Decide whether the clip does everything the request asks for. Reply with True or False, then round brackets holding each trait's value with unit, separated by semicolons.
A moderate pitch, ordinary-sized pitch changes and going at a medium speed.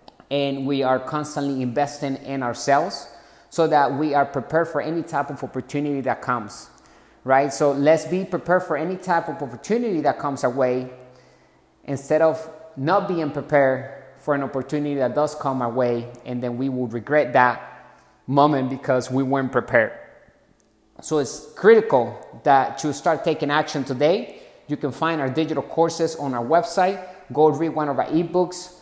True (145 Hz; 3.2 semitones; 170 wpm)